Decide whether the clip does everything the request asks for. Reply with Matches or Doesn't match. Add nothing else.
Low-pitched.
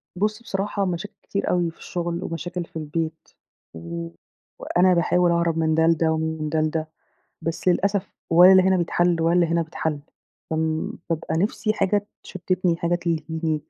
Doesn't match